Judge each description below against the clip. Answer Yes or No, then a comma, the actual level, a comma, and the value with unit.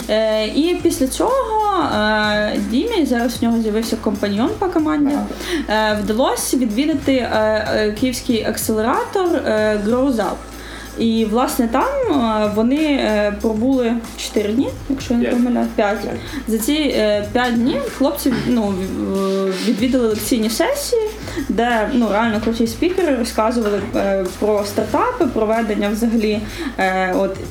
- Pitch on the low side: No, high, 235 Hz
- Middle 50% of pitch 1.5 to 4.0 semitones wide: No, average, 4.6 semitones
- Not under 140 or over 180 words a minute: No, average, 115 wpm